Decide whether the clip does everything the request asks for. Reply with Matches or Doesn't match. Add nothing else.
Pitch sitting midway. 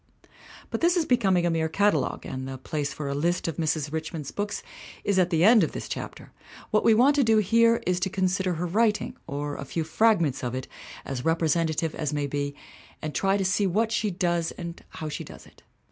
Matches